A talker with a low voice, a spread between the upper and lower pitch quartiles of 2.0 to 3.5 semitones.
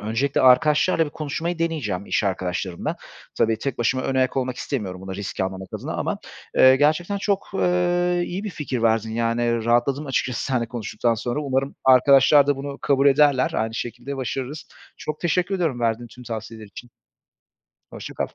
No: low, 130 Hz; average, 4.7 semitones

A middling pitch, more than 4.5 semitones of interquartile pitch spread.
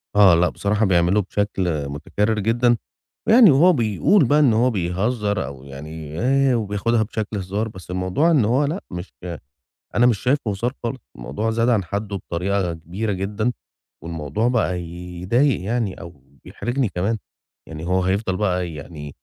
No: low, 100 Hz; average, 4.9 semitones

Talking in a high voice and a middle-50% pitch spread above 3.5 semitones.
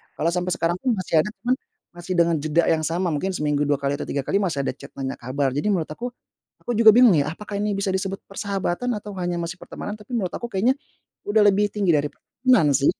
No: medium, 180 Hz; average, 5.3 semitones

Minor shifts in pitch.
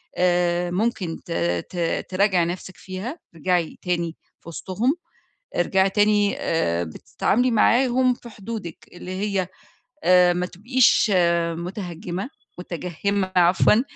No: average, 3.2 semitones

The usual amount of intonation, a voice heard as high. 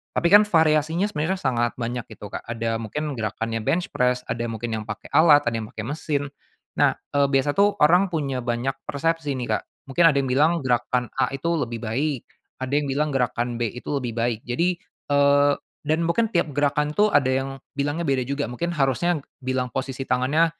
No: average, 4.2 semitones; medium, 140 Hz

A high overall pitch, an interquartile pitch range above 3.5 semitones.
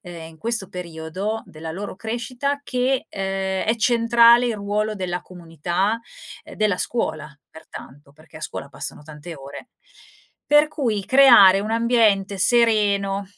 Yes: high, 200 Hz; average, 4.8 semitones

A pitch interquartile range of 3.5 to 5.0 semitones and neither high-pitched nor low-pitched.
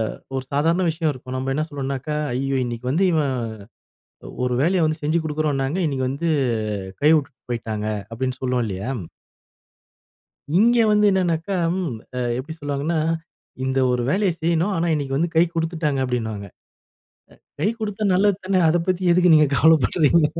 Yes: average, 4.4 semitones; medium, 155 Hz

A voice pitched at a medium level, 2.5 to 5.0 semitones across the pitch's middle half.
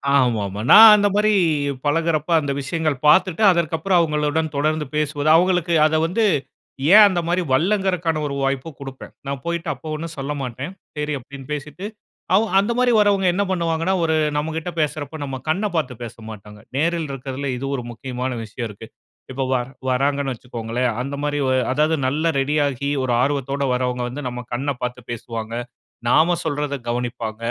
Yes: medium, 145 Hz; average, 4.2 semitones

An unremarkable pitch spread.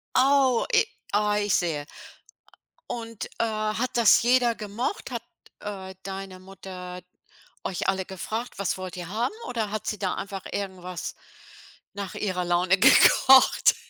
Yes: average, 3.5 semitones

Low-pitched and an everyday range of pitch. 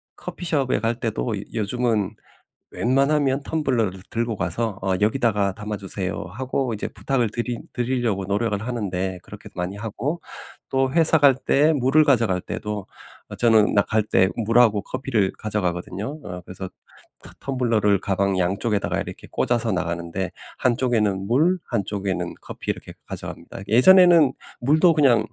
Yes: low, 115 Hz; average, 4.7 semitones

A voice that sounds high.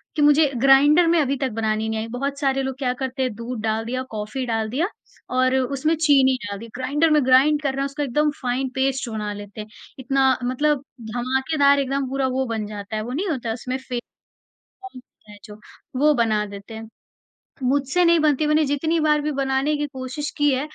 Yes: very high, 265 Hz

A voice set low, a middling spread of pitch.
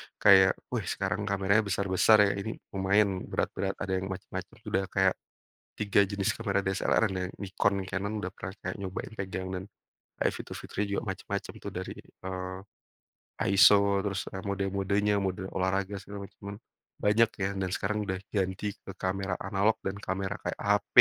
No: very low, 95 Hz; narrow, 1.2 semitones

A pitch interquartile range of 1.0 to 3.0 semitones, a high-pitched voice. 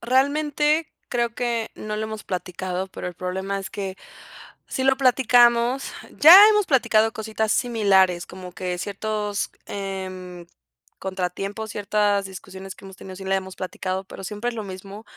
No: average, 3.8 semitones; high, 200 Hz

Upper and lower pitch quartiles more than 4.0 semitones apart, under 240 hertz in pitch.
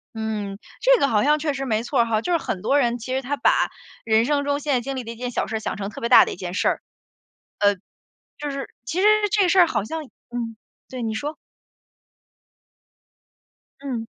No: average, 4.6 semitones; very high, 250 Hz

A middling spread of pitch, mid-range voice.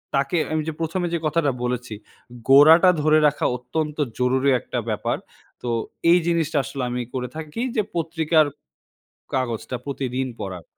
Yes: average, 4.1 semitones; medium, 145 Hz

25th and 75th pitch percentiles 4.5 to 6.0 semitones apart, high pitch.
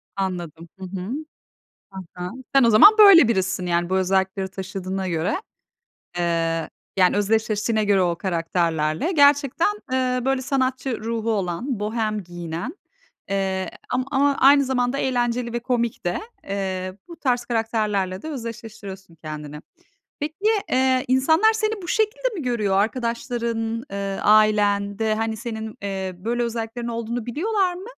Yes: average, 5.2 semitones; high, 220 Hz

